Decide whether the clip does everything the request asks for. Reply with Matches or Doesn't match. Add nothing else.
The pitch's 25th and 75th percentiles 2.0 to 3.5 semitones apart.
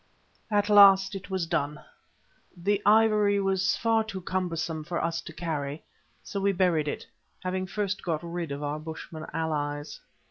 Doesn't match